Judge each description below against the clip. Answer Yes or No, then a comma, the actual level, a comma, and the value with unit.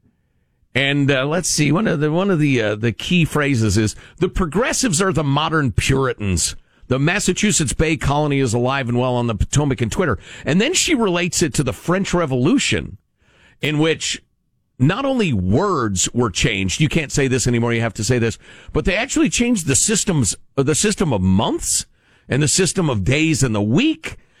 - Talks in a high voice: No, medium, 140 Hz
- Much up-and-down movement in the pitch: Yes, wide, 6.9 semitones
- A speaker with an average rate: Yes, average, 190 wpm